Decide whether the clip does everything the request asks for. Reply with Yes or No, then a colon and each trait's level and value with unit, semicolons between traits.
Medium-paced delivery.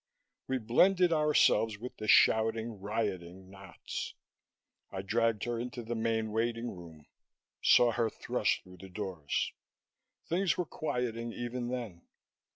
No: slow, 130 wpm